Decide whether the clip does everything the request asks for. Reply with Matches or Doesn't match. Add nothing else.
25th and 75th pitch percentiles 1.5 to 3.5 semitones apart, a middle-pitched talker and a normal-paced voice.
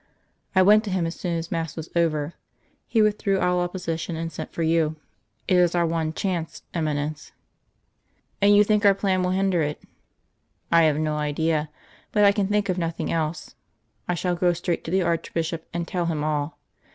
Matches